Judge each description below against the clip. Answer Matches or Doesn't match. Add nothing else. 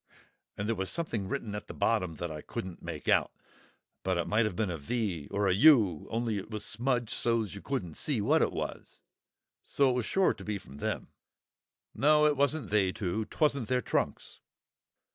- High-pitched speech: Doesn't match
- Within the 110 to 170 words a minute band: Doesn't match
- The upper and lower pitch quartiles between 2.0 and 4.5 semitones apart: Doesn't match